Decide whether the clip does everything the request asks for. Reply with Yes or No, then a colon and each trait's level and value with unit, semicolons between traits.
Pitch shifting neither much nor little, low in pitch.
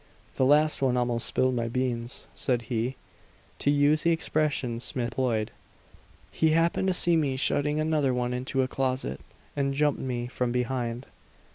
Yes: average, 3.3 semitones; low, 130 Hz